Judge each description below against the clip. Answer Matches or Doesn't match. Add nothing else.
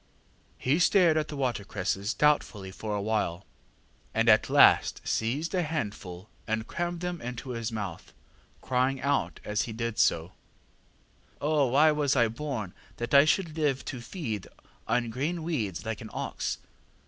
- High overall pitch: Doesn't match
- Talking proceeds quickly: Doesn't match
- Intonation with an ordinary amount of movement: Doesn't match